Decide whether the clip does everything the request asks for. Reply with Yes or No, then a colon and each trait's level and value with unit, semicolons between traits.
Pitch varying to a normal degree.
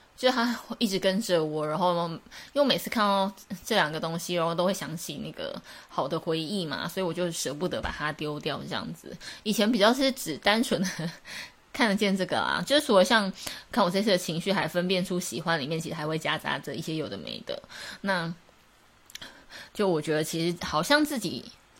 Yes: average, 4.0 semitones